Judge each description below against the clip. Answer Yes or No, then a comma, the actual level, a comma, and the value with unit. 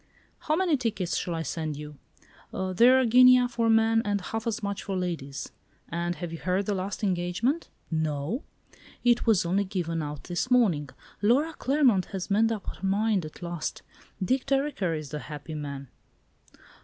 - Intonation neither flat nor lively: No, wide, 5.9 semitones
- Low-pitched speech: No, high, 195 Hz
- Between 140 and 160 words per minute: No, average, 170 wpm